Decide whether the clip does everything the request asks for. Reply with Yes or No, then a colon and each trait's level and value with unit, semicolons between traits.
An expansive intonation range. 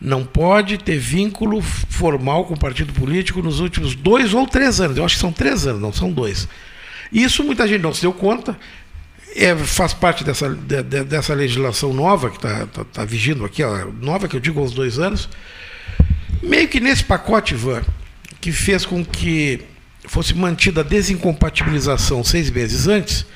Yes: wide, 6.7 semitones